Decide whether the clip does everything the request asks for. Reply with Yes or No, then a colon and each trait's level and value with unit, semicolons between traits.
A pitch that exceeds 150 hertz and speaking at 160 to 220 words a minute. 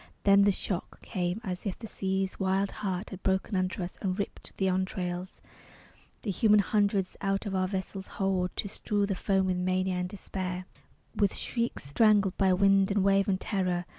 Yes: high, 190 Hz; average, 185 wpm